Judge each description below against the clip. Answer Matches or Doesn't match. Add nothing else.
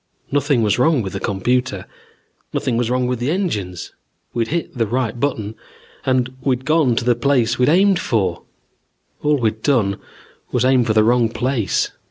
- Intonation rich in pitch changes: Doesn't match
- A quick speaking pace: Doesn't match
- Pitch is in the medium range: Doesn't match